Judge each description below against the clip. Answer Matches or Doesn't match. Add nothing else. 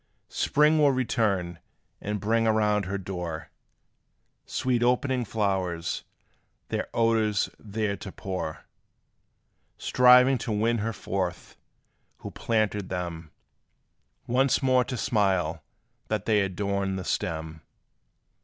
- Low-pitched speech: Matches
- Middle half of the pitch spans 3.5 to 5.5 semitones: Matches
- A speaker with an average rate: Doesn't match